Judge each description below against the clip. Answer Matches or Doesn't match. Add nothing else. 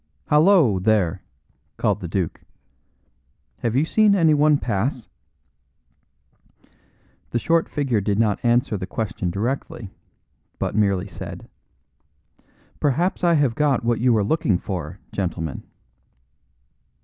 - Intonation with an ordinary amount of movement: Doesn't match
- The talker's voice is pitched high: Doesn't match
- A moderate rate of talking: Doesn't match